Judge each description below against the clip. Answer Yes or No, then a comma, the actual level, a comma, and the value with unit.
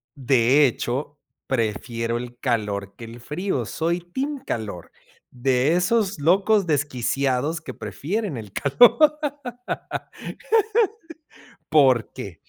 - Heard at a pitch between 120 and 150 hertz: Yes, low, 135 Hz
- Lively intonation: Yes, wide, 6.9 semitones